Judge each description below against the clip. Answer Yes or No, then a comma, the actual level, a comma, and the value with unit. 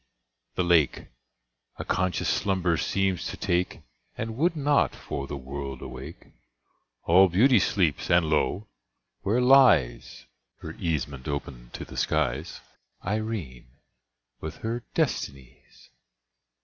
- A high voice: No, very low, 85 Hz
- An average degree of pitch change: No, wide, 7.4 semitones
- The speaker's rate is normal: No, slow, 110 wpm